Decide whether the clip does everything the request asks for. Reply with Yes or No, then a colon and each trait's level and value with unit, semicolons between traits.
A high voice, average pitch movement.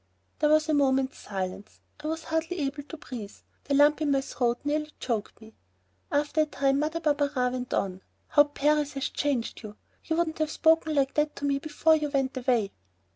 Yes: very high, 285 Hz; average, 3.0 semitones